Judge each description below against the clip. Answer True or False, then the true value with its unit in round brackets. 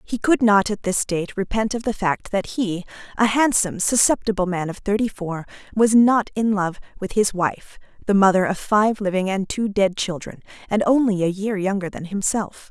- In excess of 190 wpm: True (200 wpm)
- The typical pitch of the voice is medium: False (205 Hz)